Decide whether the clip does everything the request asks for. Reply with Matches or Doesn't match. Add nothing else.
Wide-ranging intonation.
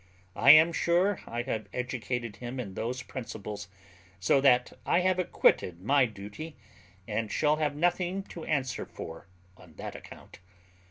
Matches